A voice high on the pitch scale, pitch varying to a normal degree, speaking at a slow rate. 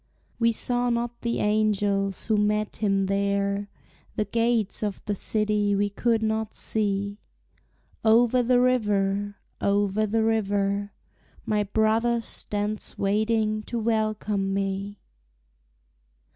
No: high, 210 Hz; narrow, 1.8 semitones; slow, 115 wpm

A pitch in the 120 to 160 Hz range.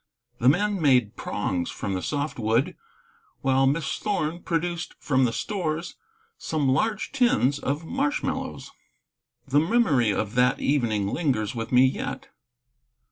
Yes: medium, 140 Hz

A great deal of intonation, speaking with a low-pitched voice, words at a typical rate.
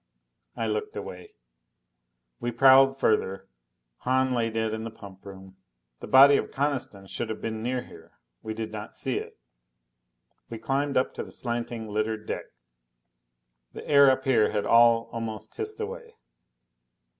No: average, 3.4 semitones; low, 115 Hz; average, 155 wpm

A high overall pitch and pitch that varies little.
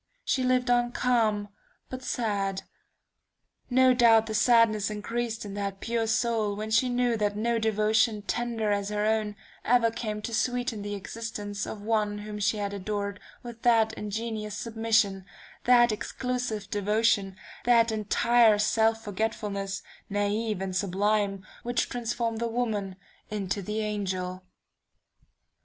Yes: high, 215 Hz; narrow, 2.2 semitones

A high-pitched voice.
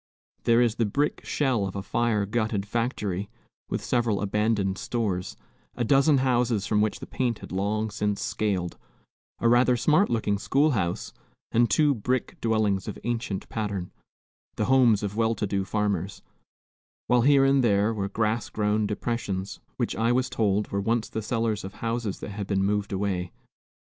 No: low, 110 Hz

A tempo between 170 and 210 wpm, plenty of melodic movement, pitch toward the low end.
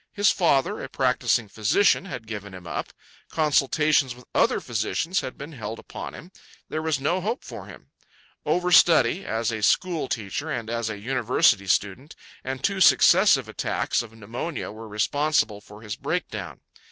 No: average, 160 wpm; wide, 6.4 semitones; low, 125 Hz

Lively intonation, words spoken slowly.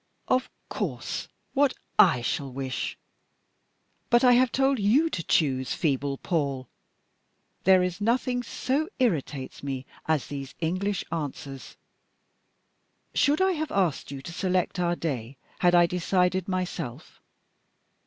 Yes: wide, 8.6 semitones; slow, 125 wpm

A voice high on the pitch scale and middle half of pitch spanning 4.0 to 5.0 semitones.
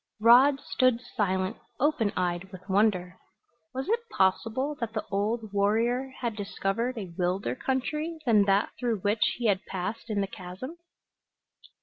Yes: high, 220 Hz; average, 4.7 semitones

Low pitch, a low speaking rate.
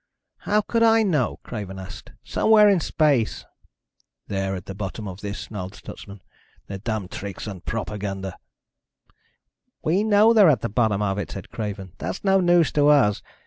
No: low, 105 Hz; average, 165 wpm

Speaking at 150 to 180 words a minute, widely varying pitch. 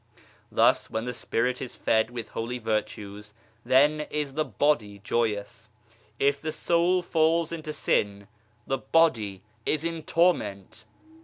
No: slow, 135 wpm; wide, 6.2 semitones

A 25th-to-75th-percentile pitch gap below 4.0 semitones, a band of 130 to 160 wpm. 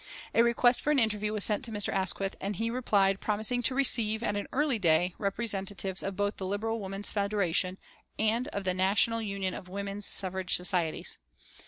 No: average, 2.7 semitones; average, 185 wpm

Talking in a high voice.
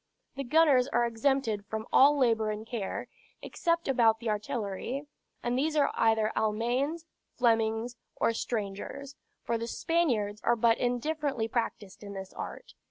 Yes: high, 235 Hz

